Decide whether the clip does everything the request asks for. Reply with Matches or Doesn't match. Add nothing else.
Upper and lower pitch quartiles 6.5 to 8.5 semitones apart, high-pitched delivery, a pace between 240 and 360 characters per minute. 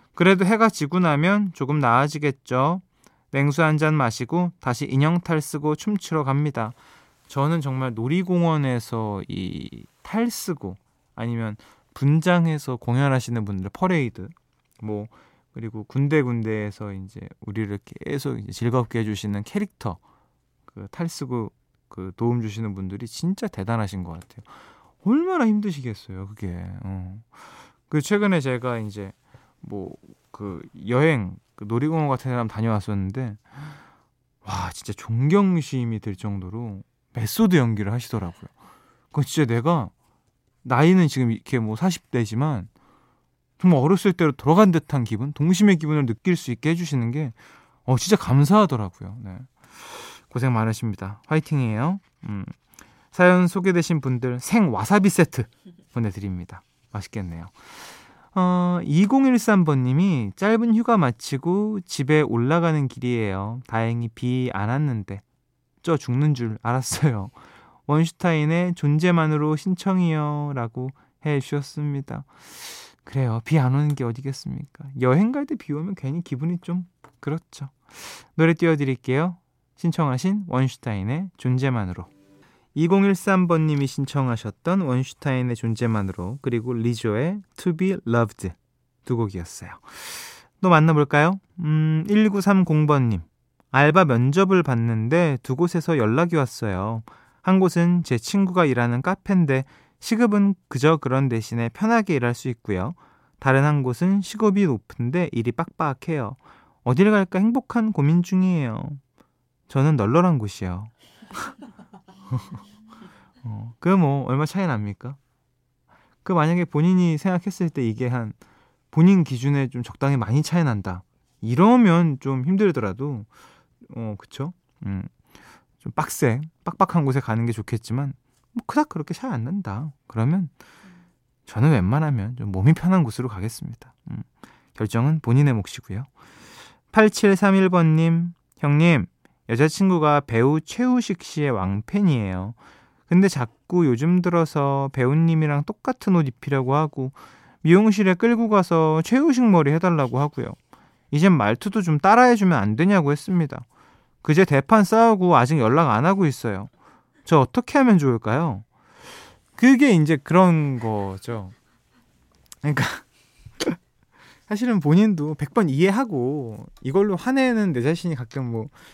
Doesn't match